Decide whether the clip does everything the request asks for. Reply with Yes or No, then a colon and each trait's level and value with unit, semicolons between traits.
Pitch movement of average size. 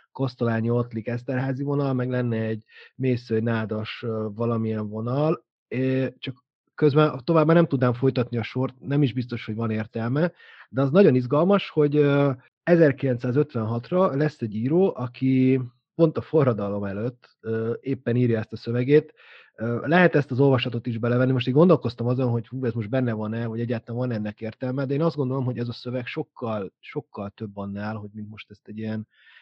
Yes: average, 3.5 semitones